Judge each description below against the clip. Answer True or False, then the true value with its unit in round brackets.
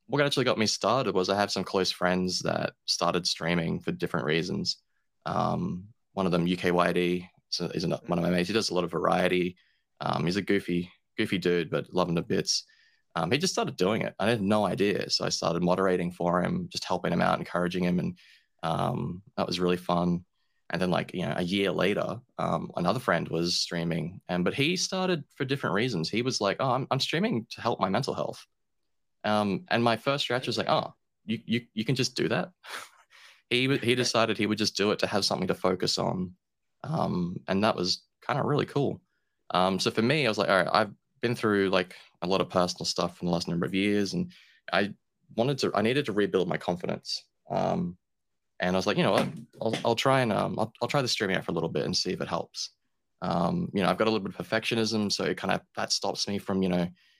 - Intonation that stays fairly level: False (5.1 semitones)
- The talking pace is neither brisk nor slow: False (235 wpm)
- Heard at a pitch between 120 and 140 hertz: False (100 Hz)